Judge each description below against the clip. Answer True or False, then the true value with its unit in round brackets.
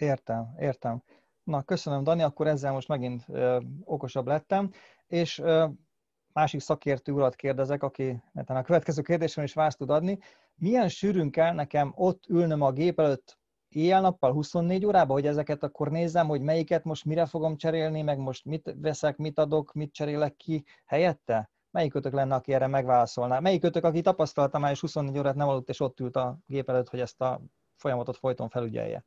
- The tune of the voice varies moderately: True (3.2 semitones)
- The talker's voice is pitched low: False (150 Hz)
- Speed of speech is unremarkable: False (175 wpm)